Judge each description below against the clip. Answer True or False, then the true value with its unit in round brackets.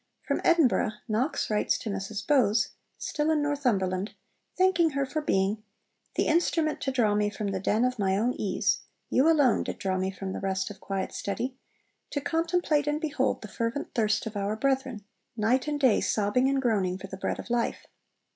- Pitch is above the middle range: True (230 Hz)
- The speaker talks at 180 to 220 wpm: True (190 wpm)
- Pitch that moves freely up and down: True (6.2 semitones)